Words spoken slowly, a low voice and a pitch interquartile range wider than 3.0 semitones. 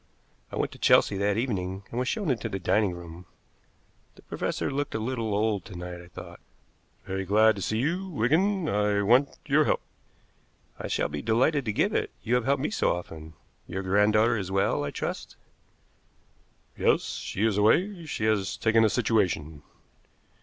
No: average, 180 wpm; low, 110 Hz; average, 4.9 semitones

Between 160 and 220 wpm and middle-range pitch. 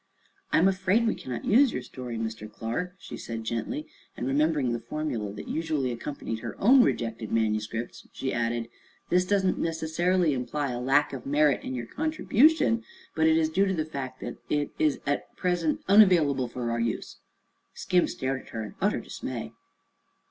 Yes: average, 175 wpm; medium, 145 Hz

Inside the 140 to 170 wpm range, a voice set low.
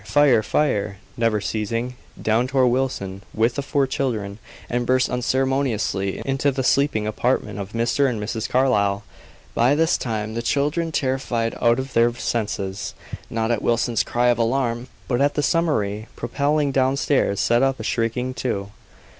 Yes: average, 155 wpm; low, 120 Hz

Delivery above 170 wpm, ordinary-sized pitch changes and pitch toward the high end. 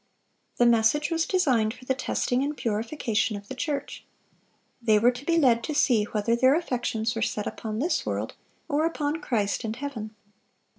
Yes: average, 180 wpm; average, 4.7 semitones; high, 245 Hz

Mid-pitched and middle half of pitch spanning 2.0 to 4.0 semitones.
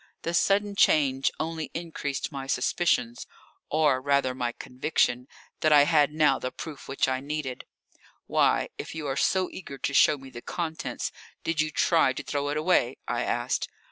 Yes: medium, 145 Hz; average, 3.1 semitones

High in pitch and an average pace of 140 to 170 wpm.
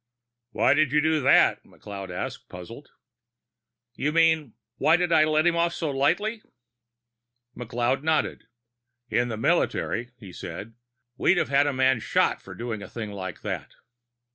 No: low, 135 Hz; average, 150 wpm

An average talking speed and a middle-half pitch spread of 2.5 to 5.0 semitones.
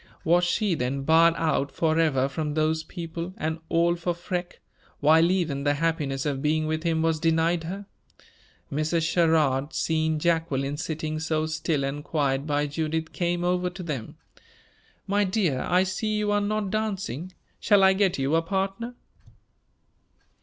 Yes: average, 155 wpm; average, 2.8 semitones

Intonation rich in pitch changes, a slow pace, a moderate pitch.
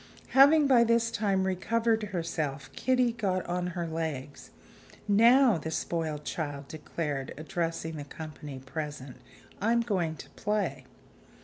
Yes: wide, 6.8 semitones; slow, 125 wpm; medium, 170 Hz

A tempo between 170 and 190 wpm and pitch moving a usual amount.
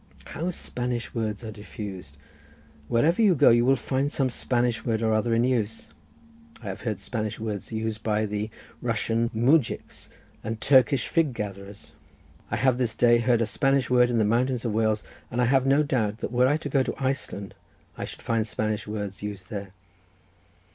Yes: average, 180 wpm; average, 3.0 semitones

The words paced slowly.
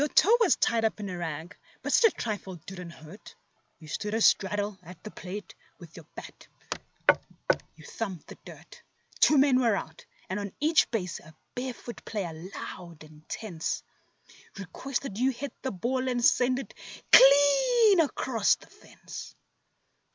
No: average, 165 wpm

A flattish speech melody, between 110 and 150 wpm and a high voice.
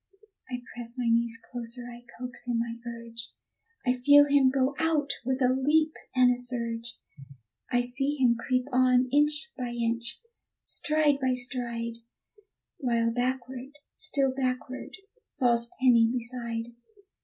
Yes: narrow, 2.0 semitones; slow, 135 wpm; very high, 250 Hz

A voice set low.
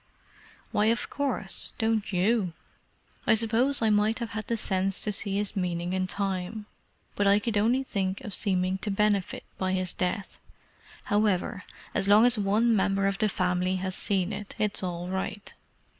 No: high, 200 Hz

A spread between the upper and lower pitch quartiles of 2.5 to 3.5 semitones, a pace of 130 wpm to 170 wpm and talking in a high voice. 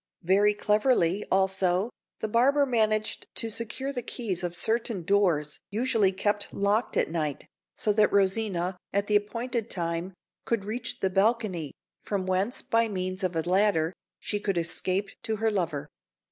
Yes: average, 3.2 semitones; average, 155 wpm; high, 200 Hz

